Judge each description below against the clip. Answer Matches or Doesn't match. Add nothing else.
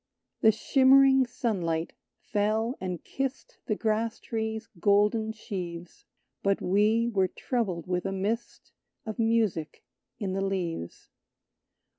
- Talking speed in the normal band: Doesn't match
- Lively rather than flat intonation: Doesn't match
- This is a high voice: Matches